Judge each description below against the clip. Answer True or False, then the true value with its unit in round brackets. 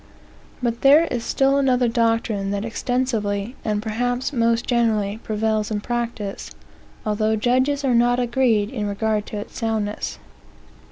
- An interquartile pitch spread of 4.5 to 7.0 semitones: False (2.6 semitones)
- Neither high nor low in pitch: False (230 Hz)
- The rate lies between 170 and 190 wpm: False (135 wpm)